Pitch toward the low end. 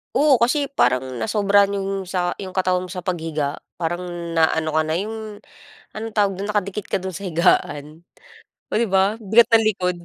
No: high, 190 Hz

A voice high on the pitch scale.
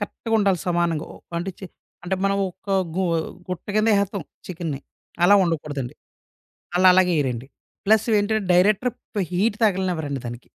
No: medium, 180 Hz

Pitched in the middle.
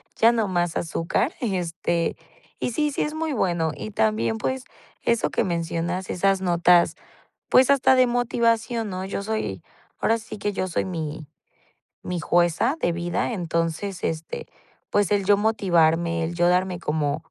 Yes: medium, 180 Hz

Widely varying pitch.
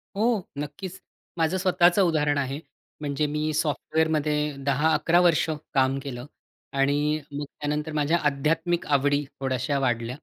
No: narrow, 2.4 semitones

